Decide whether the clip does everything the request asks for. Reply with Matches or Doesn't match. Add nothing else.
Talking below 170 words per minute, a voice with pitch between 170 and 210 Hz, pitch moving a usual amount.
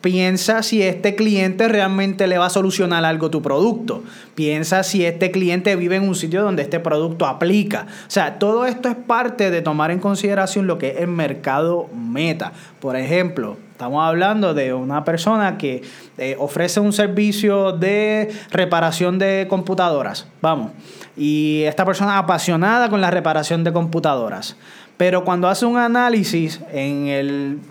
Matches